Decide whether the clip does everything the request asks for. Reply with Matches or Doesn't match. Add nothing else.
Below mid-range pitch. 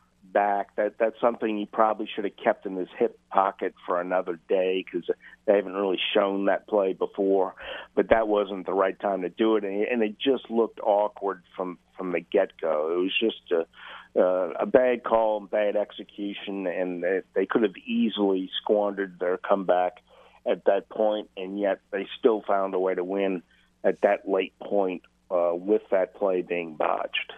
Matches